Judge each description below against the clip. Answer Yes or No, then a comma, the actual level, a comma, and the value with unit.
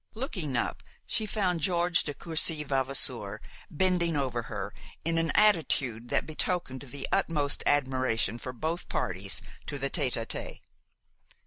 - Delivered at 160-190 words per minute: No, average, 140 wpm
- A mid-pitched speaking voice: Yes, medium, 145 Hz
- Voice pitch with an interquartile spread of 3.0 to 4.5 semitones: No, average, 4.9 semitones